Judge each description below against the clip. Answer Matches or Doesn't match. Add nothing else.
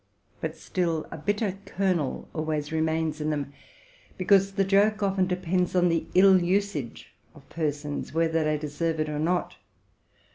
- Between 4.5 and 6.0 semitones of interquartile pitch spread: Doesn't match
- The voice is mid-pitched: Matches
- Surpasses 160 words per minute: Doesn't match